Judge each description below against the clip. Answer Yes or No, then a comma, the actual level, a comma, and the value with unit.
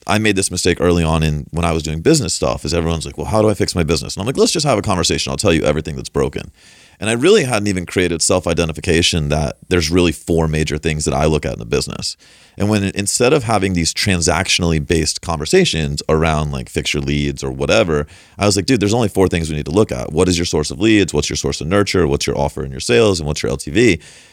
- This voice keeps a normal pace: No, fast, 265 wpm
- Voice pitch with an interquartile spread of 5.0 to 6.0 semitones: No, average, 3.9 semitones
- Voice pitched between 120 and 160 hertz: No, very low, 85 Hz